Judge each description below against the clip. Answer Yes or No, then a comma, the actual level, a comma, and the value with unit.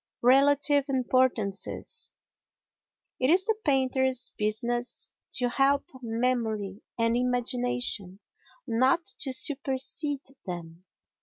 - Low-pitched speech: No, very high, 250 Hz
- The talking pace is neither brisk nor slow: No, slow, 85 wpm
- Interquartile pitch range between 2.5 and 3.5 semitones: Yes, average, 2.9 semitones